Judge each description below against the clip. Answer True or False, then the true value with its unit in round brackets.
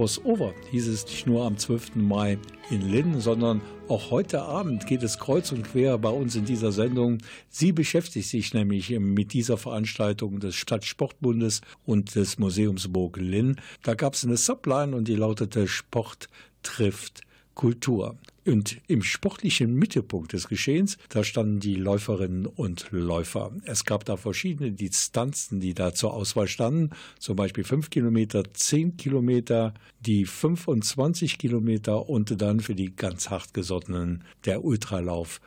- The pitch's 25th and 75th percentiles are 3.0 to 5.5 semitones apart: True (3.6 semitones)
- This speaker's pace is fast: False (150 wpm)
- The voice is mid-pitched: False (110 Hz)